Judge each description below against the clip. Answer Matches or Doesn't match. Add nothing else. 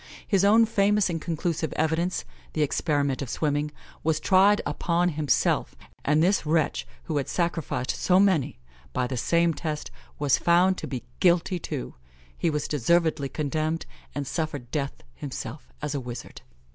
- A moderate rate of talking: Matches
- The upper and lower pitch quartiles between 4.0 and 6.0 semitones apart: Doesn't match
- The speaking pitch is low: Doesn't match